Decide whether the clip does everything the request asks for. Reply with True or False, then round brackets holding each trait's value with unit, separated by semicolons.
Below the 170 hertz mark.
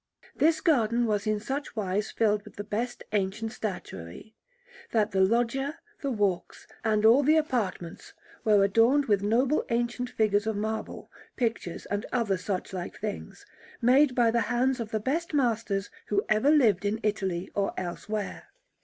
False (220 Hz)